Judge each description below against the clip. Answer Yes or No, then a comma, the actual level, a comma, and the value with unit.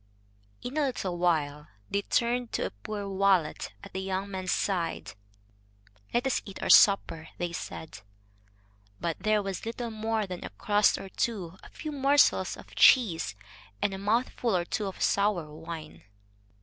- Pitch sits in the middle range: No, high, 195 Hz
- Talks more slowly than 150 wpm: No, average, 160 wpm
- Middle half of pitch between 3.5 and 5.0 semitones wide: Yes, average, 4.5 semitones